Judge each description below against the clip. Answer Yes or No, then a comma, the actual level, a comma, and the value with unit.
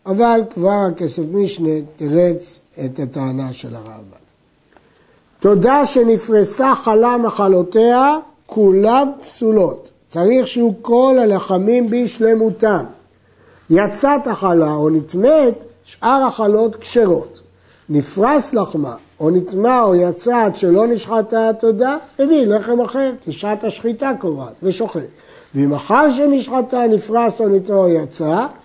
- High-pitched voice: Yes, high, 220 Hz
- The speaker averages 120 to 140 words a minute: No, average, 105 wpm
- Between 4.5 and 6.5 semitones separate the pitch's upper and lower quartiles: Yes, wide, 5.4 semitones